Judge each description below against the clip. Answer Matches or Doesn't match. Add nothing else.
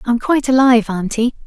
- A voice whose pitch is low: Doesn't match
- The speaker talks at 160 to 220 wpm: Matches